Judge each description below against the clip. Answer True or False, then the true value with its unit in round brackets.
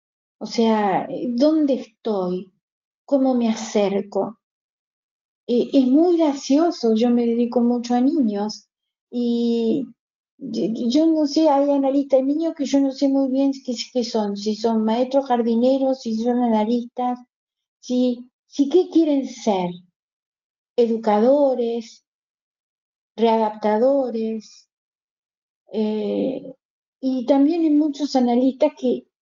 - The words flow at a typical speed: False (115 wpm)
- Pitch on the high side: True (245 Hz)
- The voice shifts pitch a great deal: False (3.5 semitones)